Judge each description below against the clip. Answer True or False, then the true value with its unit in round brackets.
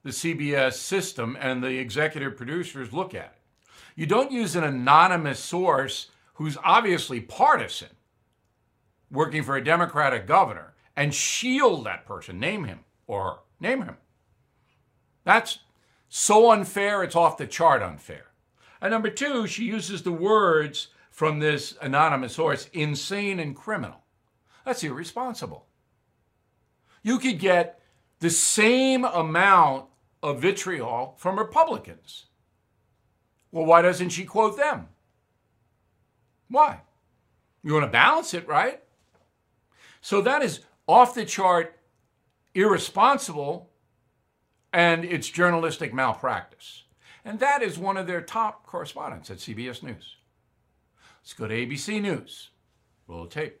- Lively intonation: True (7.2 semitones)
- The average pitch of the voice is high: False (165 Hz)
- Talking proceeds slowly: True (125 wpm)